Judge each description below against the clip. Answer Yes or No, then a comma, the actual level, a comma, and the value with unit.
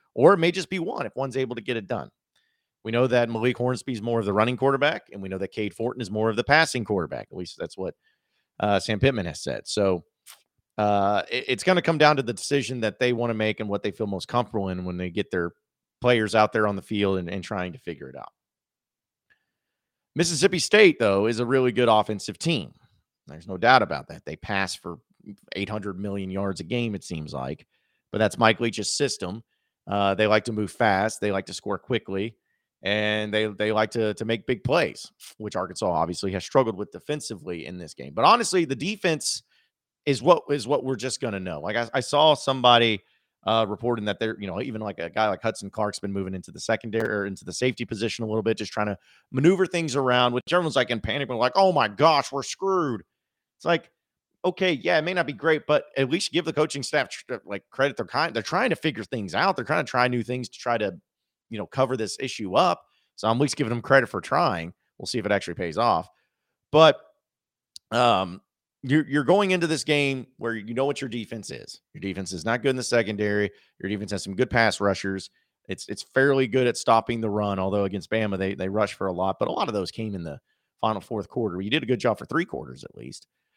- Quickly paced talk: Yes, fast, 235 wpm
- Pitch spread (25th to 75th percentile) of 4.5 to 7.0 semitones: Yes, average, 4.8 semitones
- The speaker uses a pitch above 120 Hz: No, low, 115 Hz